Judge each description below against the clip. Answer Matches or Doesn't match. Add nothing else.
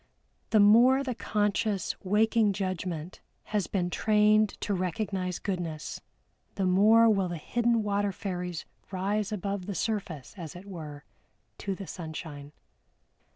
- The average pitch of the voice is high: Matches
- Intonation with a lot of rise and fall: Doesn't match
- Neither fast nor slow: Doesn't match